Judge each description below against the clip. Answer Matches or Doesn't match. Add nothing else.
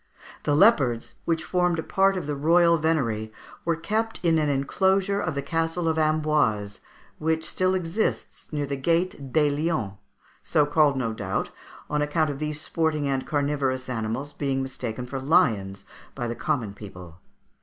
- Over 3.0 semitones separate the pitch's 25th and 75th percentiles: Matches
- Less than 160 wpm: Doesn't match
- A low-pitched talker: Doesn't match